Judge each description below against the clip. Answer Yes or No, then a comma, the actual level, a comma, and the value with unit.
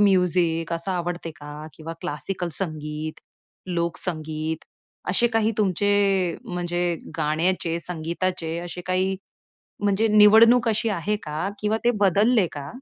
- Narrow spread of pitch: No, average, 3.8 semitones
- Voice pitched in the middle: Yes, medium, 175 Hz